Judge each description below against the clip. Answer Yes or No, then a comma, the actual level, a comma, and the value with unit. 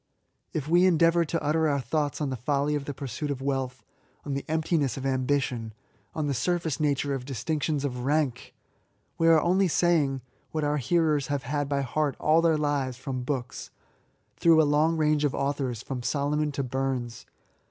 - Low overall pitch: No, medium, 145 Hz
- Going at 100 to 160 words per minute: No, average, 190 wpm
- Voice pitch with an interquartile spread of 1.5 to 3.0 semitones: Yes, average, 2.7 semitones